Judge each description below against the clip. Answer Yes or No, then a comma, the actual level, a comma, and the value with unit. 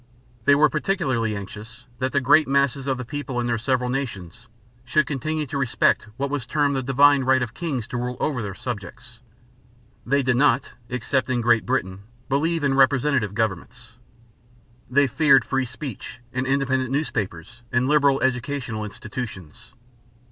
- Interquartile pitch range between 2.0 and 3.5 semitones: Yes, average, 2.9 semitones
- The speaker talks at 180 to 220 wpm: No, average, 160 wpm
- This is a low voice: Yes, low, 130 Hz